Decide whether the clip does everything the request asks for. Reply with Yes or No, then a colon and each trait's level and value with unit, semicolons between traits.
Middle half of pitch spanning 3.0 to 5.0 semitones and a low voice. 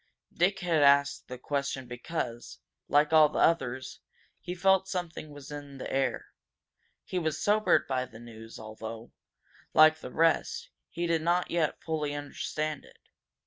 No: average, 4.2 semitones; medium, 150 Hz